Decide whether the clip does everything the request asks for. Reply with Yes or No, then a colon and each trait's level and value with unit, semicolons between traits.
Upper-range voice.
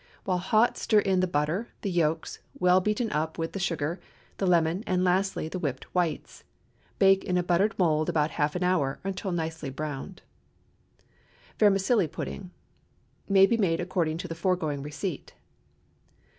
No: medium, 180 Hz